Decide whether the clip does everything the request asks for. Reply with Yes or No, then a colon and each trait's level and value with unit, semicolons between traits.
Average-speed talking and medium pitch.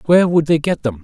No: fast, 290 wpm; medium, 150 Hz